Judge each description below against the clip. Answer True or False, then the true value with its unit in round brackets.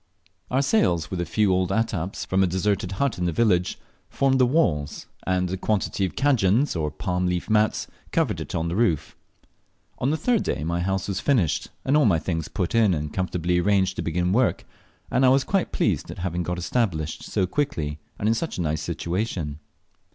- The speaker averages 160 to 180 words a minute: False (200 wpm)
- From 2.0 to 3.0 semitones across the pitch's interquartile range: False (4.8 semitones)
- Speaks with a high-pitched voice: False (95 Hz)